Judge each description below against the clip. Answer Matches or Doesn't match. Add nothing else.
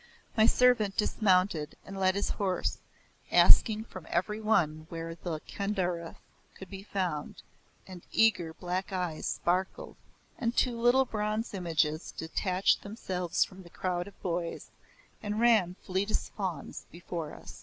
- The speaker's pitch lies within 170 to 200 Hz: Matches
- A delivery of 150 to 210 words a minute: Doesn't match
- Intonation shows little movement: Doesn't match